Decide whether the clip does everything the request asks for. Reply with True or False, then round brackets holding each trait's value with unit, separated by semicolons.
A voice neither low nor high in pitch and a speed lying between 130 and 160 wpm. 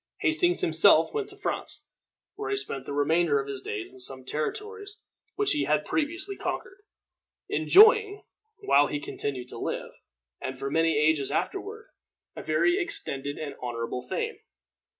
True (165 Hz; 155 wpm)